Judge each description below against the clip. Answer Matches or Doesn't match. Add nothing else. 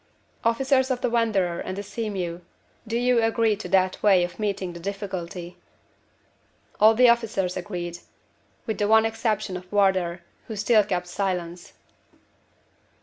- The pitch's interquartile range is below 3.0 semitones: Doesn't match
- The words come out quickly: Doesn't match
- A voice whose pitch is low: Doesn't match